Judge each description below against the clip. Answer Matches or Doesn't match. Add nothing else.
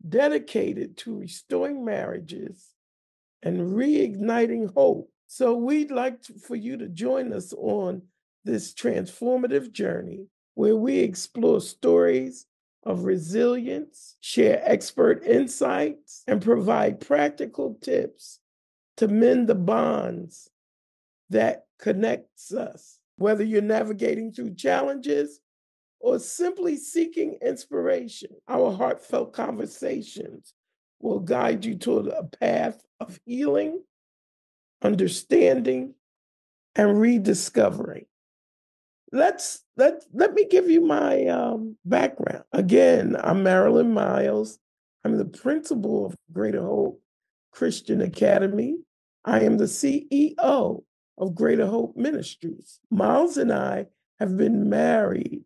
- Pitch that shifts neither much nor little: Doesn't match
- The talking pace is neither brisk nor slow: Doesn't match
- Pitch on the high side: Matches